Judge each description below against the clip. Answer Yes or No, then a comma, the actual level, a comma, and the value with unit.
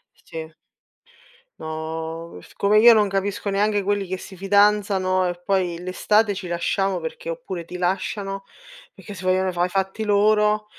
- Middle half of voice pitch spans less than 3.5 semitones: Yes, narrow, 2.4 semitones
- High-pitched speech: Yes, high, 195 Hz